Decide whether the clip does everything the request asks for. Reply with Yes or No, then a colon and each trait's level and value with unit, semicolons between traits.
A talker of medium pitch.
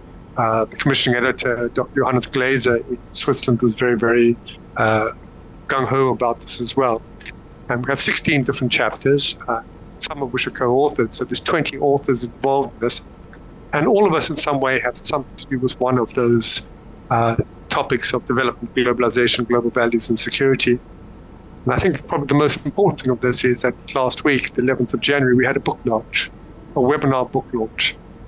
No: low, 125 Hz